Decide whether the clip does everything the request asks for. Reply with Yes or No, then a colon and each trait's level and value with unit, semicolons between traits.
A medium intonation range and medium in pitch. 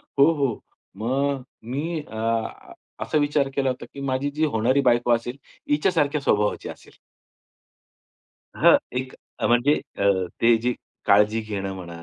No: average, 4.0 semitones; low, 130 Hz